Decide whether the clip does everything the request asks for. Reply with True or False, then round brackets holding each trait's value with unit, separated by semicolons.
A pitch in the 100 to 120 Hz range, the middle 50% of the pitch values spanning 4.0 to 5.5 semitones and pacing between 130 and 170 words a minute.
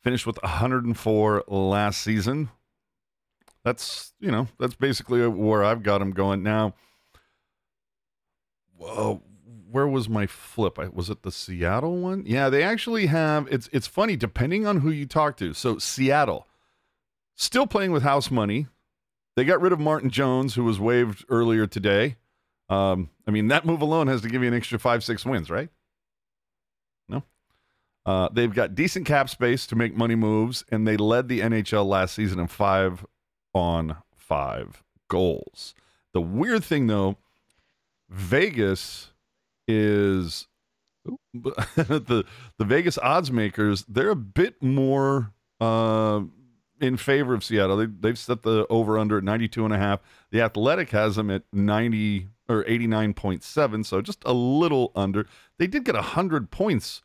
True (115 Hz; 4.3 semitones; 155 wpm)